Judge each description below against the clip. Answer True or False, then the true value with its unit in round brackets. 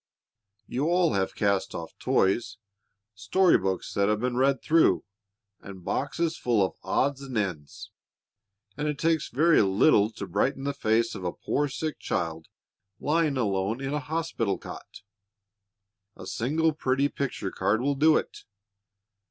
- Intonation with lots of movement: True (6.8 semitones)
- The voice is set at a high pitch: False (125 Hz)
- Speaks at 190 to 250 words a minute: False (150 wpm)